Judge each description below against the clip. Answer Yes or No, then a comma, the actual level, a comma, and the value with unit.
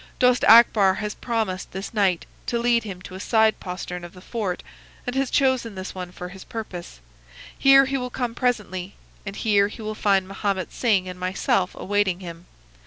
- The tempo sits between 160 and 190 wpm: Yes, average, 185 wpm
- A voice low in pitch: No, high, 200 Hz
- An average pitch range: Yes, average, 4.0 semitones